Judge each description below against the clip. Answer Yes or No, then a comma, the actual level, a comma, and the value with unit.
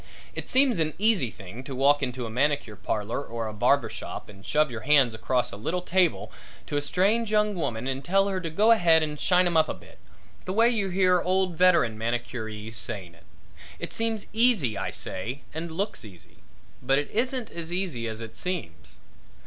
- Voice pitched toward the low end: No, medium, 150 Hz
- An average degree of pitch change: No, wide, 8.3 semitones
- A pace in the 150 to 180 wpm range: No, average, 200 wpm